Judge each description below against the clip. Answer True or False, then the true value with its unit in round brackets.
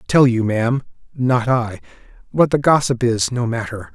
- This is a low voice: True (125 Hz)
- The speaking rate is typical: True (150 wpm)